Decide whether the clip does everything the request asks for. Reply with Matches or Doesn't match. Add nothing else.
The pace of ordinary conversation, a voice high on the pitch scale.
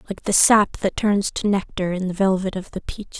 Doesn't match